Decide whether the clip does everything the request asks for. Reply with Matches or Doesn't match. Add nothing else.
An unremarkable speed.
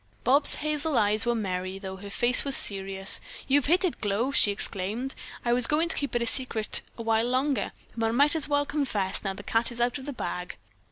Doesn't match